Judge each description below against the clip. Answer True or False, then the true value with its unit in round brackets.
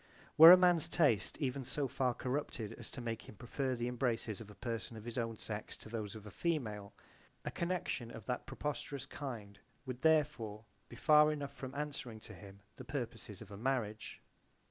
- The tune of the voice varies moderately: True (4.6 semitones)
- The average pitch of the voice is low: True (120 Hz)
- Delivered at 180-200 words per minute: True (190 wpm)